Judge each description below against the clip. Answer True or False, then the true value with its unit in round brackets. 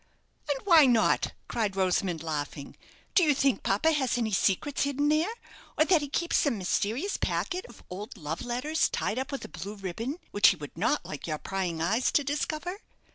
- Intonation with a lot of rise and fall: True (7.6 semitones)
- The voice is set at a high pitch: True (240 Hz)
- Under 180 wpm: False (190 wpm)